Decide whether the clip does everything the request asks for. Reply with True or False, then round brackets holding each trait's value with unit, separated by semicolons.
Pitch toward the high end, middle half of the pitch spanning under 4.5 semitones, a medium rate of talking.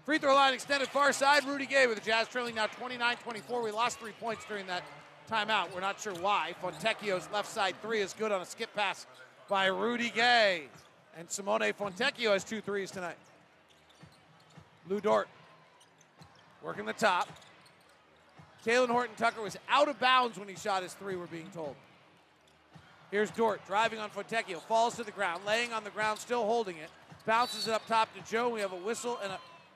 True (215 Hz; 3.7 semitones; 190 wpm)